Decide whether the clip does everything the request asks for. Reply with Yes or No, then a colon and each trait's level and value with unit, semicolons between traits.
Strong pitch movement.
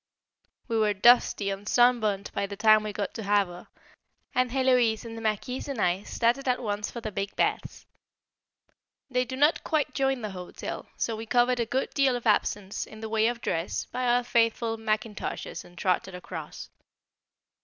No: average, 3.2 semitones